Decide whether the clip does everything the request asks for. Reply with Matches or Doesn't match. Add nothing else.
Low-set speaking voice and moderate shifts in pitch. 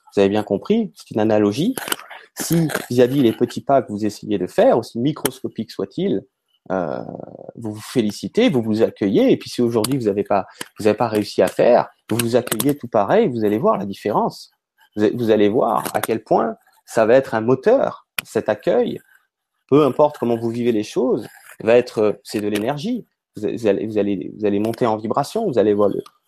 Matches